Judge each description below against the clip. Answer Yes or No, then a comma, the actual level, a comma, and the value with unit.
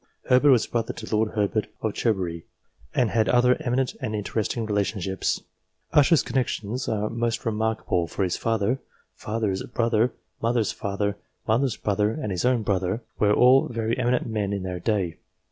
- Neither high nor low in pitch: No, low, 110 Hz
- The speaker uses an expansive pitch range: No, average, 2.9 semitones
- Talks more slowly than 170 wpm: Yes, average, 160 wpm